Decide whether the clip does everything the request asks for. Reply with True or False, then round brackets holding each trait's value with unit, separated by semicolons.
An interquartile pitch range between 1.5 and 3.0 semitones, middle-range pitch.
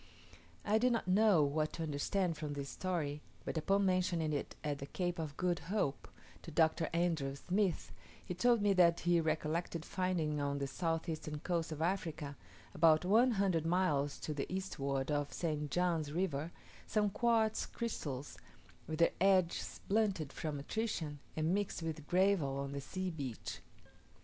False (3.9 semitones; 165 Hz)